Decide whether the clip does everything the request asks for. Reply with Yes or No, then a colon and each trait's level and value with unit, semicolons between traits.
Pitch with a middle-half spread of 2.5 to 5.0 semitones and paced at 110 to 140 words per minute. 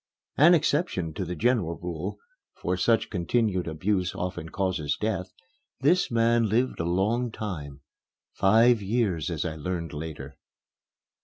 No: wide, 5.5 semitones; slow, 135 wpm